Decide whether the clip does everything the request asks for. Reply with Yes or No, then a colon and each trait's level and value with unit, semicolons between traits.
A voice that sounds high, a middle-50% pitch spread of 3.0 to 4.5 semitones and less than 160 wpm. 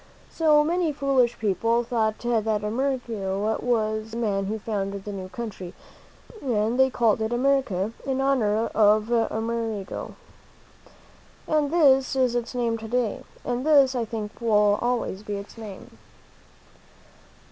Yes: high, 230 Hz; average, 3.3 semitones; slow, 135 wpm